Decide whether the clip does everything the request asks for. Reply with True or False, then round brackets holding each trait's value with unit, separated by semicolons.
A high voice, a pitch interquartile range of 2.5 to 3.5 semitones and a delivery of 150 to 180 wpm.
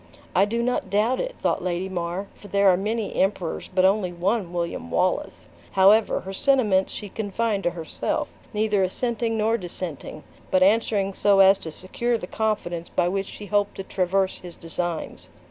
True (195 Hz; 2.9 semitones; 175 wpm)